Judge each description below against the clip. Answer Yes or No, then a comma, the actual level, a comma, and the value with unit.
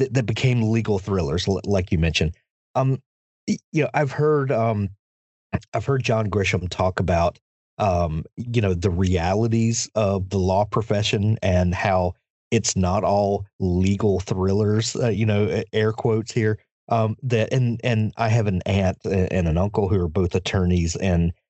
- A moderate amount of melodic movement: Yes, average, 3.6 semitones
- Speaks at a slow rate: No, average, 160 wpm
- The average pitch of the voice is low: Yes, low, 105 Hz